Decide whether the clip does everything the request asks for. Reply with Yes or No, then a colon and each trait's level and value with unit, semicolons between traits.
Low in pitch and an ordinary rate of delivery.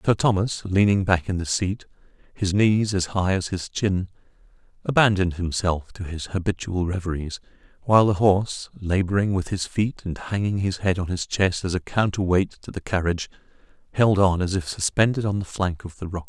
Yes: very low, 95 Hz; average, 190 wpm